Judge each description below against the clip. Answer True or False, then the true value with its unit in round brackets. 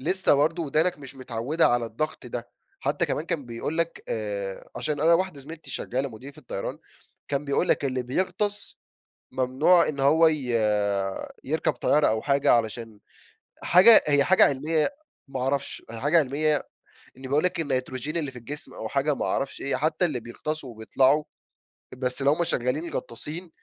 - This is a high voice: False (140 Hz)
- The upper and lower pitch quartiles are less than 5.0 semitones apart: True (3.8 semitones)